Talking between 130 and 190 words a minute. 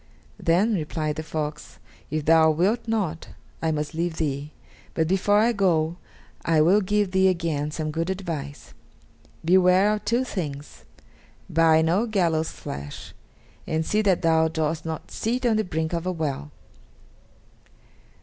Yes: average, 150 wpm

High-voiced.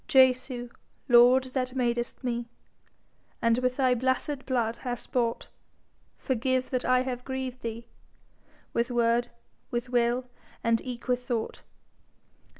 Yes: high, 245 Hz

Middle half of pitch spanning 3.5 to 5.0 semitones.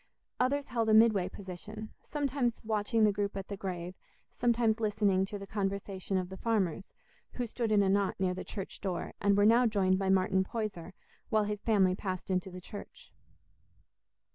No: narrow, 2.6 semitones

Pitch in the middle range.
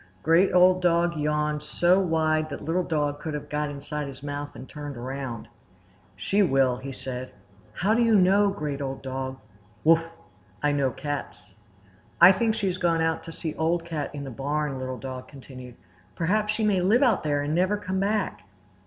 Yes: medium, 150 Hz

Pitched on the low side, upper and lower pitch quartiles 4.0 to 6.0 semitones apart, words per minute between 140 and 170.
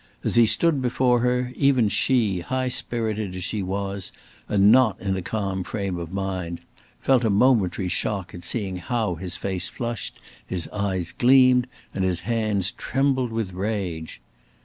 Yes: low, 100 Hz; average, 4.7 semitones; average, 160 wpm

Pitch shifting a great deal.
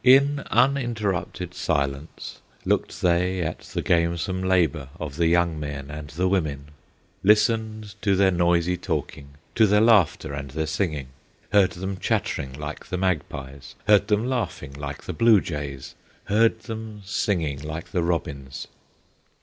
Yes: wide, 5.9 semitones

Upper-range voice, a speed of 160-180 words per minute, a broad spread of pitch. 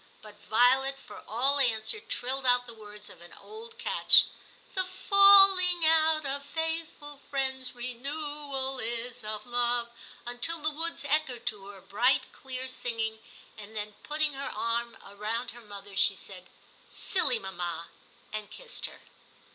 No: very high, 255 Hz; average, 150 wpm; wide, 5.7 semitones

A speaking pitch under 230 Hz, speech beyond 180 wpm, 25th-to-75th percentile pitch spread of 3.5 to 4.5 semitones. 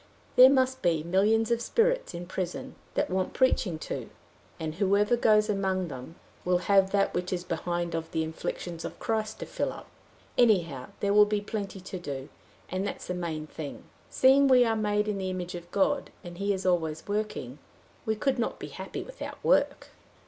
Yes: high, 190 Hz; average, 190 wpm; average, 3.9 semitones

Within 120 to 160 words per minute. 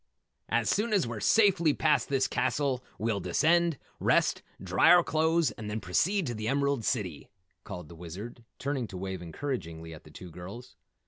No: average, 175 wpm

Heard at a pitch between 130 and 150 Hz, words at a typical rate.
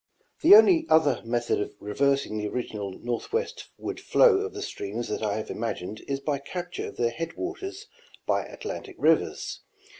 Yes: medium, 140 Hz; average, 160 wpm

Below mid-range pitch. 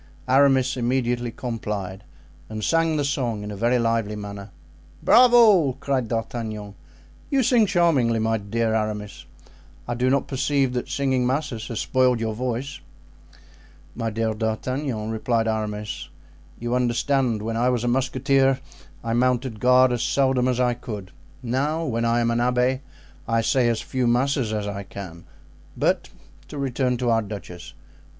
Yes: low, 120 Hz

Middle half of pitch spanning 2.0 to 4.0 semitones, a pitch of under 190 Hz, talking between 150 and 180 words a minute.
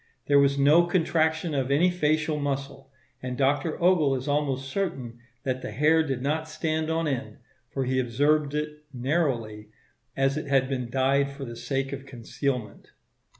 Yes: average, 2.8 semitones; medium, 140 Hz; average, 165 wpm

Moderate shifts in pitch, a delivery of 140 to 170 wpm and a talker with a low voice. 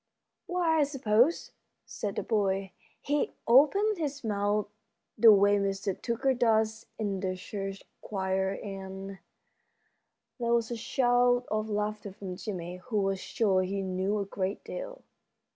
No: average, 3.8 semitones; average, 145 wpm; high, 210 Hz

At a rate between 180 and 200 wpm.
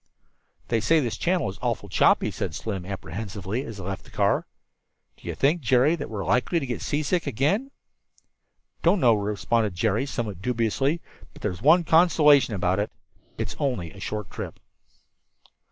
No: average, 170 wpm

